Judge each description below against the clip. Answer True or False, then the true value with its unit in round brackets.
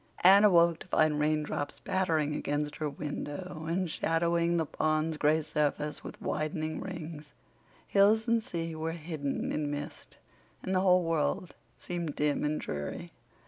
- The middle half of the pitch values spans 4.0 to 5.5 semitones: False (2.4 semitones)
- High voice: False (160 Hz)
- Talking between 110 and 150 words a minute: True (145 wpm)